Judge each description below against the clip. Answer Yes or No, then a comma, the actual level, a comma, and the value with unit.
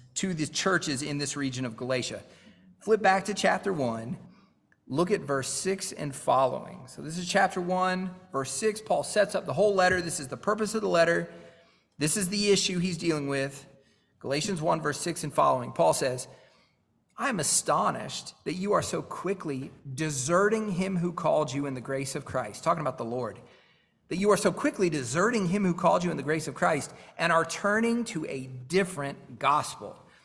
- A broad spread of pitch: Yes, wide, 5.7 semitones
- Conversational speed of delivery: Yes, average, 195 wpm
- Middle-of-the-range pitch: Yes, medium, 165 Hz